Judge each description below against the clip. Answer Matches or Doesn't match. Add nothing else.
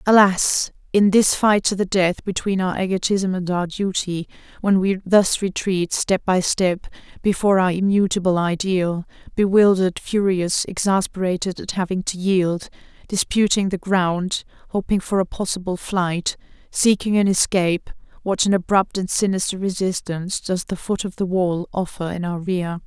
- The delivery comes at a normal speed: Matches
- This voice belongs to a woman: Matches